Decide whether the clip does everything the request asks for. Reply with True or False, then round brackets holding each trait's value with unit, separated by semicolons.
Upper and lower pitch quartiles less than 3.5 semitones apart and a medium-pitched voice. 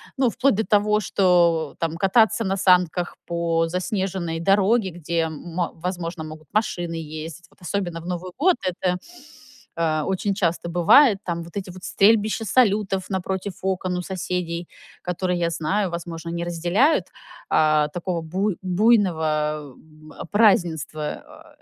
True (2.8 semitones; 180 Hz)